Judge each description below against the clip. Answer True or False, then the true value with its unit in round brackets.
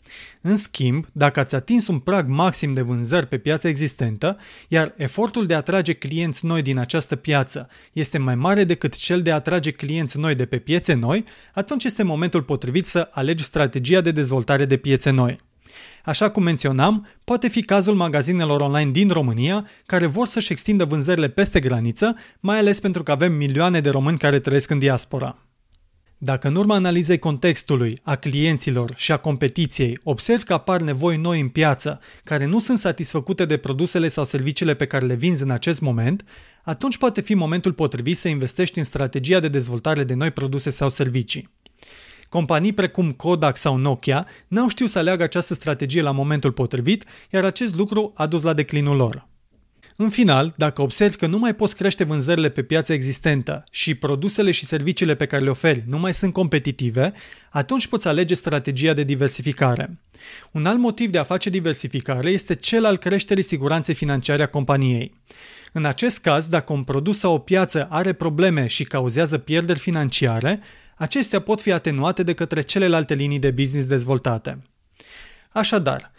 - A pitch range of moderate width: True (4.6 semitones)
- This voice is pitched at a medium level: True (155 Hz)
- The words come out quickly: True (175 wpm)